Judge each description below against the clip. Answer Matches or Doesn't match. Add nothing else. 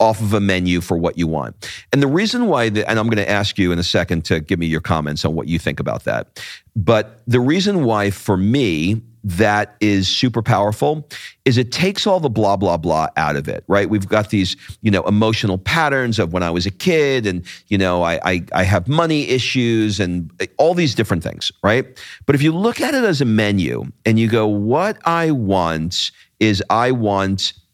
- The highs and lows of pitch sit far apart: Doesn't match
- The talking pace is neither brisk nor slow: Doesn't match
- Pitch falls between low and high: Doesn't match